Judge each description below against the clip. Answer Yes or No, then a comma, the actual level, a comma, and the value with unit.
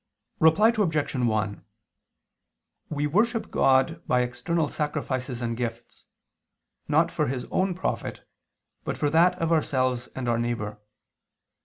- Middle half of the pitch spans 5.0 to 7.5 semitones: Yes, average, 5.3 semitones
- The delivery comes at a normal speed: No, slow, 125 wpm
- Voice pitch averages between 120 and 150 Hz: Yes, low, 135 Hz